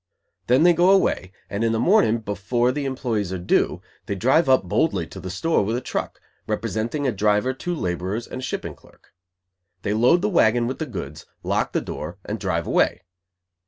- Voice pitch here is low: Yes, low, 115 Hz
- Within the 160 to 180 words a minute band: No, average, 195 wpm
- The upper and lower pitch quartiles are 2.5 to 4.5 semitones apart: No, average, 5.2 semitones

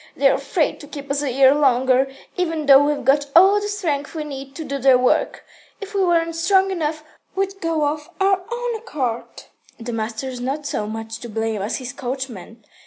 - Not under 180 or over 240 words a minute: Yes, average, 195 wpm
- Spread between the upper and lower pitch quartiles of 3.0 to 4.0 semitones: No, average, 4.6 semitones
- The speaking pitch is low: No, very high, 285 Hz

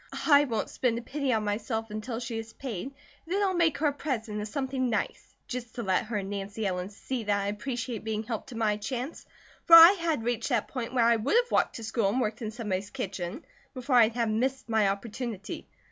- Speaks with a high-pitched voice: Yes, high, 230 Hz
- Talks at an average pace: No, fast, 230 wpm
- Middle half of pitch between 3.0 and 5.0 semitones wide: Yes, average, 3.7 semitones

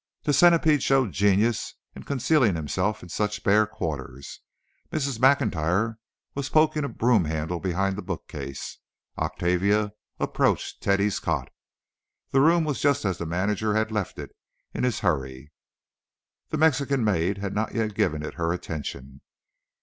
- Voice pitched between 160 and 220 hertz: No, low, 105 Hz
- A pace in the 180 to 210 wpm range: No, average, 145 wpm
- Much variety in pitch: Yes, wide, 7.0 semitones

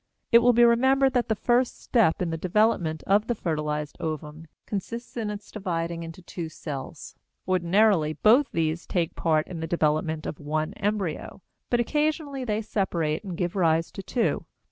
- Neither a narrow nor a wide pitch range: No, wide, 6.0 semitones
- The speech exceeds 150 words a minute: Yes, average, 170 wpm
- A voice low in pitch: No, medium, 185 Hz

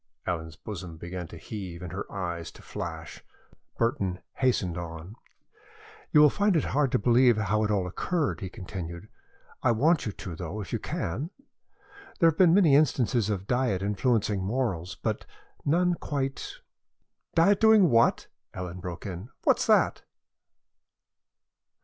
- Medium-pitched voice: No, low, 105 Hz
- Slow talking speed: No, average, 150 wpm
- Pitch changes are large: Yes, wide, 7.1 semitones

